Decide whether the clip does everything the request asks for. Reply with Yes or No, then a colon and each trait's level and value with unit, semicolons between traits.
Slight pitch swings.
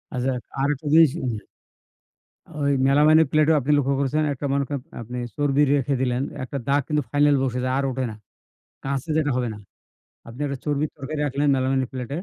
Yes: narrow, 2.0 semitones